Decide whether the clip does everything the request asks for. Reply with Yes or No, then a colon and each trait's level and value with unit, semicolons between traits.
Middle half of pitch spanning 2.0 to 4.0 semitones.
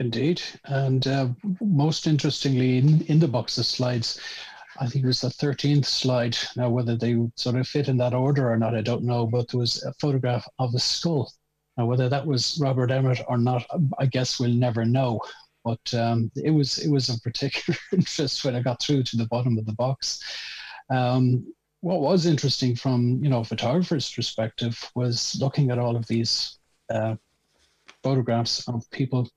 Yes: average, 2.8 semitones